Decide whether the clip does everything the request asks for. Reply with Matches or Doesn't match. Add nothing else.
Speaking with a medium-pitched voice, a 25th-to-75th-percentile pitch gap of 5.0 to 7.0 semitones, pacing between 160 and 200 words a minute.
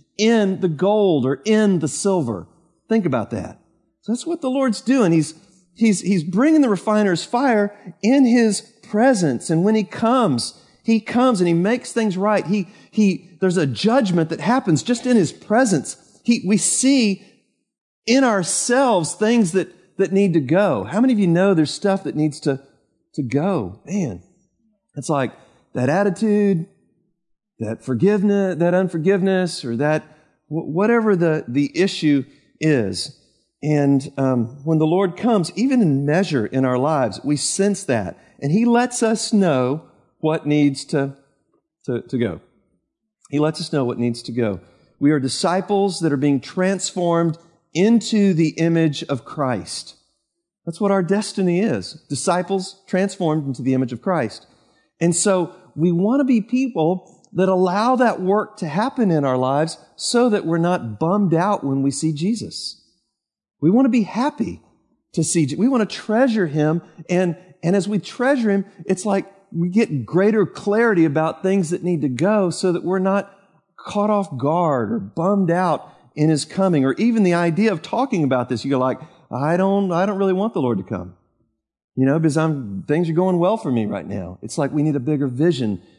Matches